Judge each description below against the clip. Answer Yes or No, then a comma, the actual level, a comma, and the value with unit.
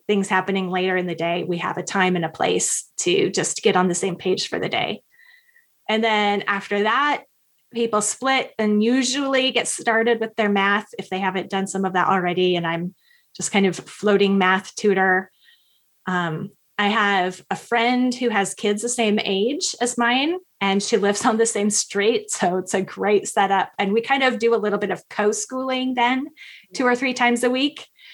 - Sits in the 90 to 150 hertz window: No, high, 210 Hz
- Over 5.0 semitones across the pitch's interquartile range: No, average, 4.2 semitones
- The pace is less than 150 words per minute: No, average, 200 wpm